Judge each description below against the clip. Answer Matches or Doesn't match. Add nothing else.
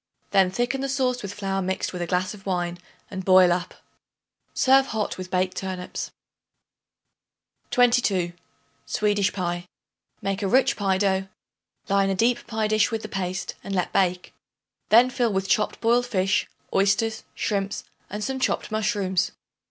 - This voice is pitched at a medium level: Doesn't match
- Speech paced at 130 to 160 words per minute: Matches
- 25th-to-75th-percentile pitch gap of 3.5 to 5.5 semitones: Doesn't match